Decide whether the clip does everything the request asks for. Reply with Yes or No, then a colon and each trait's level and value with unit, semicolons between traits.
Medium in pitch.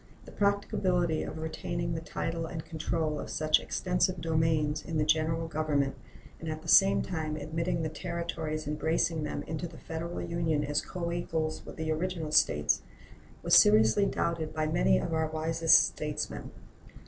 Yes: medium, 160 Hz